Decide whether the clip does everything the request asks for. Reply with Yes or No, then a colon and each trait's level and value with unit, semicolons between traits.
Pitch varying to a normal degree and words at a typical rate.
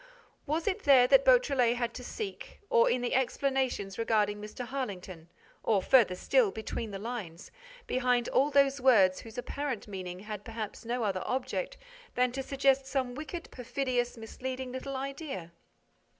Yes: average, 4.1 semitones; average, 155 wpm